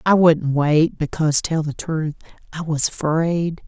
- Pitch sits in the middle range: Yes, medium, 160 Hz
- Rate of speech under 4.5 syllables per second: Yes, 4.1 syllables/s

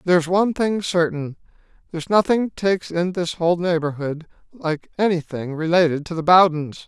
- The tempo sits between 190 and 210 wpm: No, average, 150 wpm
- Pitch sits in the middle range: Yes, medium, 170 Hz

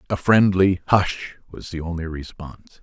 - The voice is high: No, very low, 85 Hz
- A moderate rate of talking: Yes, average, 150 wpm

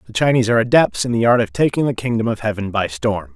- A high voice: No, low, 110 Hz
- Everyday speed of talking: No, fast, 270 wpm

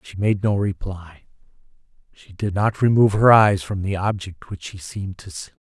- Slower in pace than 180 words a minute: No, average, 190 wpm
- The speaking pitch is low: Yes, very low, 95 Hz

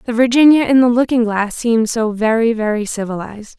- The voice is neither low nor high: No, high, 230 Hz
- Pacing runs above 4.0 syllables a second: Yes, 5.8 syllables/s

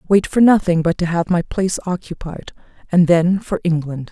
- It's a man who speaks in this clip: No, female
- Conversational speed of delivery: Yes, average, 190 wpm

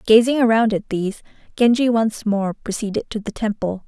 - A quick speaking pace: No, average, 170 wpm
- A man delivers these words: No, female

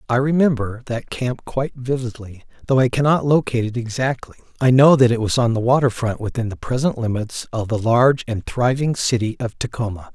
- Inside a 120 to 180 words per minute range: No, average, 195 wpm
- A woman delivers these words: No, male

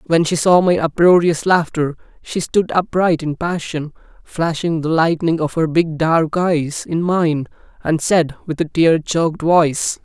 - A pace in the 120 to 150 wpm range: No, average, 165 wpm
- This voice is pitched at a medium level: Yes, medium, 165 Hz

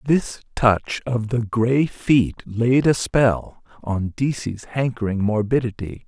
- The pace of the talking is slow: Yes, slow, 130 wpm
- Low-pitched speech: Yes, low, 120 Hz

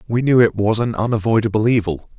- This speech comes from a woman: No, male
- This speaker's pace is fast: No, average, 190 wpm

